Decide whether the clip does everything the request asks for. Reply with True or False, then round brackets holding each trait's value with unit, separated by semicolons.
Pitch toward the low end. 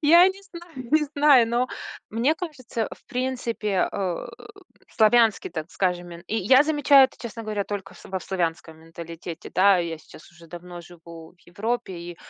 False (205 Hz)